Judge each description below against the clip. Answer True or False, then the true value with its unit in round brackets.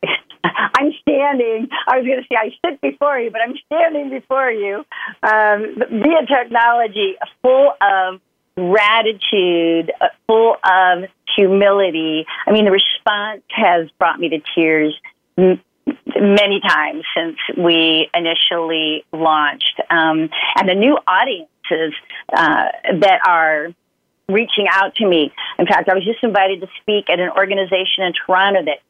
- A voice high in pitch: True (195 Hz)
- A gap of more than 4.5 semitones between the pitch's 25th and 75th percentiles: True (5.3 semitones)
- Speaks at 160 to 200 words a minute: False (135 wpm)